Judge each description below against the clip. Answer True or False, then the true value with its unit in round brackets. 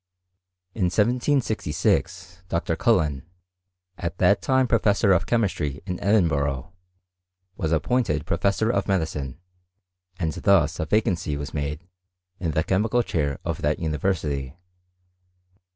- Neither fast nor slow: False (120 wpm)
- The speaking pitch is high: False (85 Hz)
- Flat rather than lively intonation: False (5.4 semitones)